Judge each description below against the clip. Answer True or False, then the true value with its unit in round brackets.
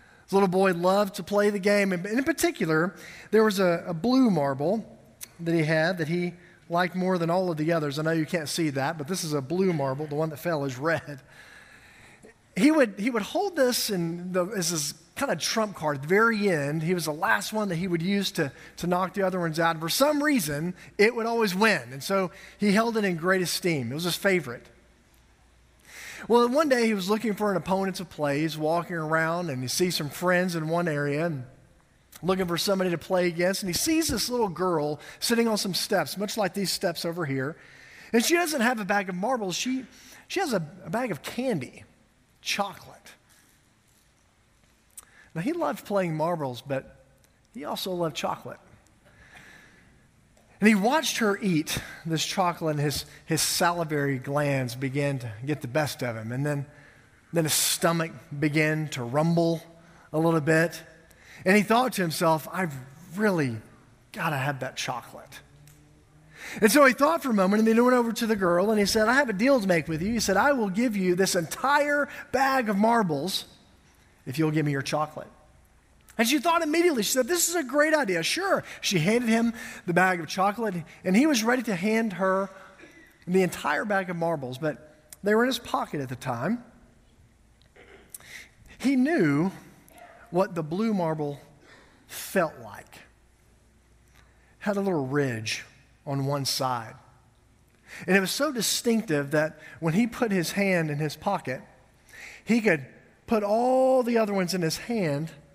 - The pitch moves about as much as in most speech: False (6.0 semitones)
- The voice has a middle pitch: True (180 Hz)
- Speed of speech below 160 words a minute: False (190 wpm)